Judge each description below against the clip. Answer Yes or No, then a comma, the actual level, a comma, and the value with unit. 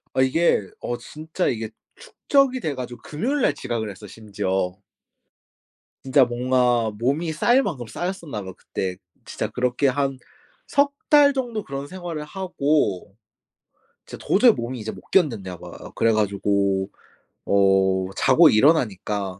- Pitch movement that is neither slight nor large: No, wide, 8.2 semitones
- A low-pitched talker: Yes, low, 125 Hz